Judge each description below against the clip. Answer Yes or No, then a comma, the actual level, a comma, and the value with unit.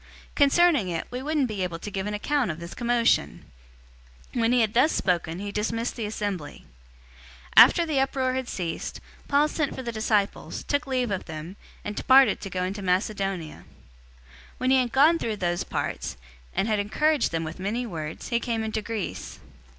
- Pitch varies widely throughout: Yes, wide, 5.8 semitones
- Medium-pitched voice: No, high, 220 Hz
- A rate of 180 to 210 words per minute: Yes, average, 190 wpm